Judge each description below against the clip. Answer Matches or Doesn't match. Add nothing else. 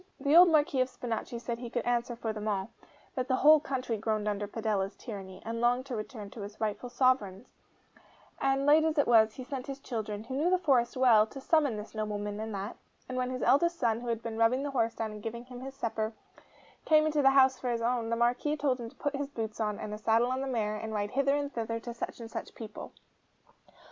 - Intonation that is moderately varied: Matches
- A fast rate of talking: Matches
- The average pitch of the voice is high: Matches